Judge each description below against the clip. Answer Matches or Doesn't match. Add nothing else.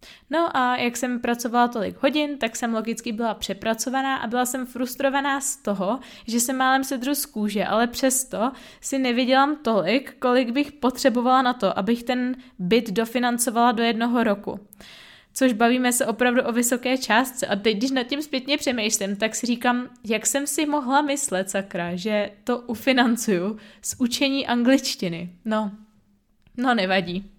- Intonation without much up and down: Doesn't match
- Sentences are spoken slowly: Doesn't match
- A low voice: Doesn't match